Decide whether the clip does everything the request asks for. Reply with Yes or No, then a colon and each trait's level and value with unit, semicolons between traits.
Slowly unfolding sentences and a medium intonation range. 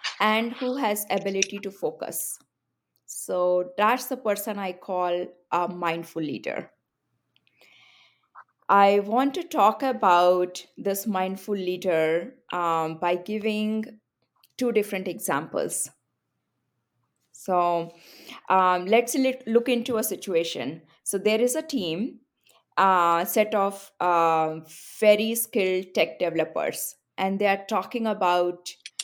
Yes: slow, 115 wpm; average, 3.6 semitones